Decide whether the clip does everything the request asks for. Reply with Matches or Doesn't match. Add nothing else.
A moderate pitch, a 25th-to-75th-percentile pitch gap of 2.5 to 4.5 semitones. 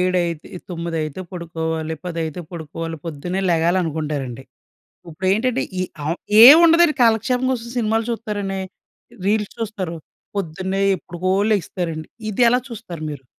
Doesn't match